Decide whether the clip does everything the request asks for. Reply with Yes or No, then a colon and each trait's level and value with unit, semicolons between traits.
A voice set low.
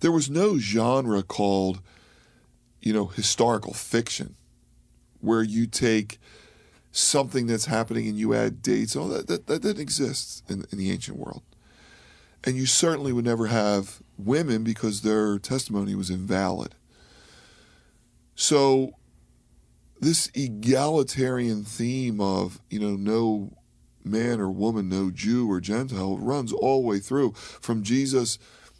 Yes: low, 110 Hz